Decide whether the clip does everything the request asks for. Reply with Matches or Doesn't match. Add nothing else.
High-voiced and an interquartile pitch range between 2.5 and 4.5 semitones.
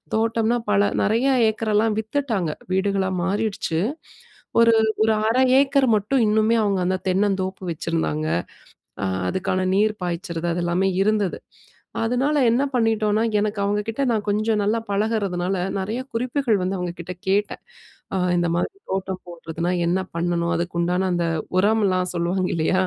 Matches